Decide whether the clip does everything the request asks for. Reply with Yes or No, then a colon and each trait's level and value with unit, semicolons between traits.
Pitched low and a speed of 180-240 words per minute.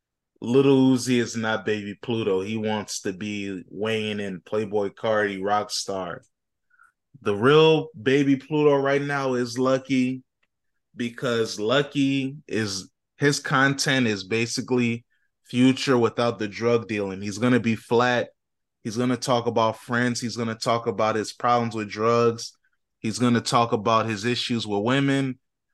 No: low, 120 Hz; average, 140 wpm